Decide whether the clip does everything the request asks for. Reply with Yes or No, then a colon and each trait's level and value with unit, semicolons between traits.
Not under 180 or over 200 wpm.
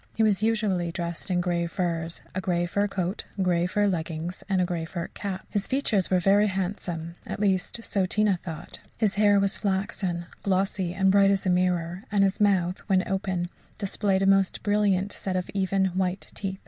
Yes: average, 190 wpm